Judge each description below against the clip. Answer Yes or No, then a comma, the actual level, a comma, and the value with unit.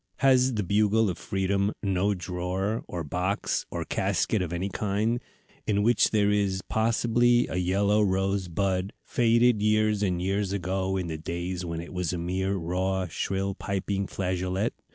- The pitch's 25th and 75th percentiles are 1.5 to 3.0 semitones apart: Yes, narrow, 2.4 semitones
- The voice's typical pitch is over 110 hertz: No, very low, 95 Hz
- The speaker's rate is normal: Yes, average, 160 wpm